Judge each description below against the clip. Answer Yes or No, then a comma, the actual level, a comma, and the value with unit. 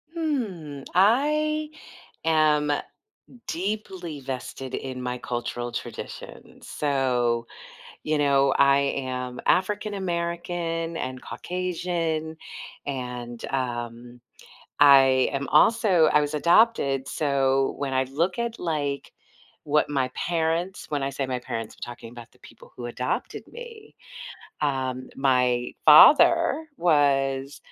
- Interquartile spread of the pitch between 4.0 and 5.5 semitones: Yes, average, 5.1 semitones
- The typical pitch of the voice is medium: Yes, medium, 145 Hz